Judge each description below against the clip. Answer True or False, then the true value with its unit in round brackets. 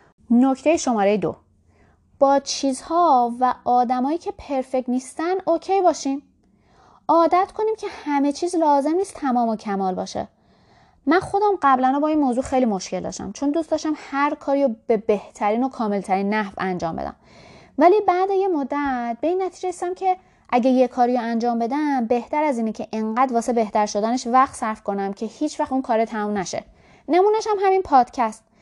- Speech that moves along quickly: True (170 wpm)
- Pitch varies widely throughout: True (5.9 semitones)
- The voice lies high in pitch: True (265 Hz)